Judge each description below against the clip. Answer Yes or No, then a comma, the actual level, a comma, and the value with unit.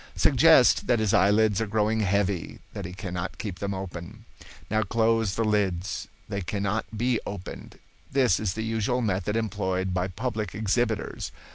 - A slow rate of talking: No, average, 155 wpm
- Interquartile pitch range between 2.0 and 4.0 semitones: Yes, average, 2.9 semitones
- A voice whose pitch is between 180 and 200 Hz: No, low, 105 Hz